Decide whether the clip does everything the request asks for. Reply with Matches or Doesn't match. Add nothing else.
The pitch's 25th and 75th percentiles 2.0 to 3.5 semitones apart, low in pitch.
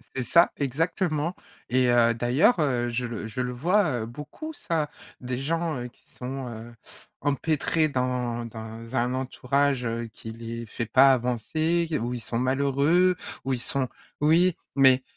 Doesn't match